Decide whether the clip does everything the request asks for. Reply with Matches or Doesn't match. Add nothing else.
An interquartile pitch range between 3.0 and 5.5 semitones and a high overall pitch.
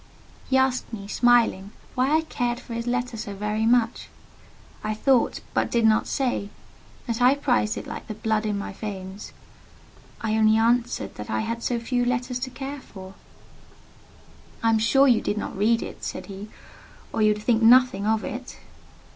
Doesn't match